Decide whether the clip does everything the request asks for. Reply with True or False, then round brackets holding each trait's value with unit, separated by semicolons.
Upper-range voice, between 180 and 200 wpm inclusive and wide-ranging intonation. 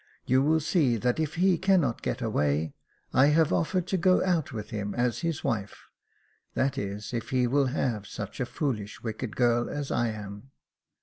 False (125 Hz; 185 wpm; 6.4 semitones)